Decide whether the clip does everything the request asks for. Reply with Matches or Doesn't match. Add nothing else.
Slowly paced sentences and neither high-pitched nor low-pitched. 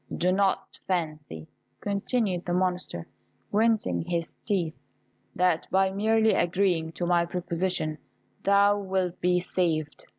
Matches